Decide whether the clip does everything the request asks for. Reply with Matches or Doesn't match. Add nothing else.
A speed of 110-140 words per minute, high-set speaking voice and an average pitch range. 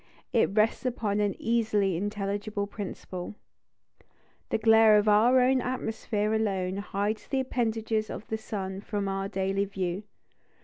Doesn't match